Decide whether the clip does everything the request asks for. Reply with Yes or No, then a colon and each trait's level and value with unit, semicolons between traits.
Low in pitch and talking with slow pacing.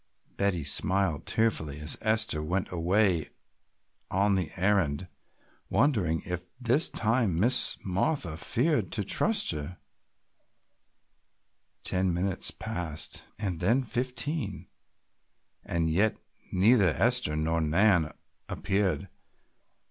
Yes: very low, 95 Hz; slow, 100 wpm